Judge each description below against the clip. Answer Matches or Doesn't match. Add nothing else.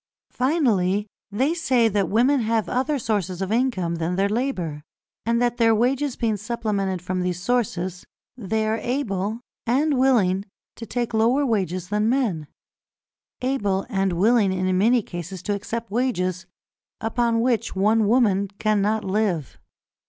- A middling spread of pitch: Matches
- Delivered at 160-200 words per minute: Doesn't match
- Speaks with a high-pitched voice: Matches